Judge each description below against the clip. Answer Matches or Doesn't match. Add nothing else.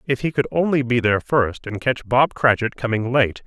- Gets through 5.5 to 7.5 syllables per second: Doesn't match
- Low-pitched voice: Matches